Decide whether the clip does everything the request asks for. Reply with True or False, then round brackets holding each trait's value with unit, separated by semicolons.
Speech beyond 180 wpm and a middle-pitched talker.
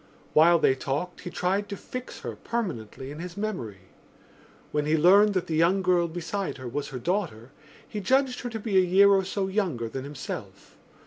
True (195 wpm; 180 Hz)